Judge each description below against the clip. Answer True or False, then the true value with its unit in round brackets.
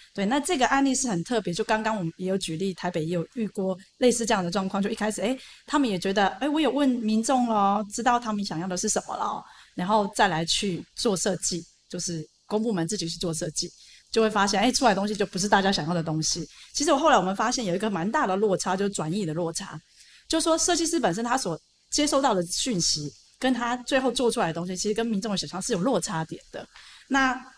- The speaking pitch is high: True (205 Hz)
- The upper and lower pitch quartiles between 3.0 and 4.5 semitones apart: False (5.3 semitones)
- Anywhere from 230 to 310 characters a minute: False (355 characters per minute)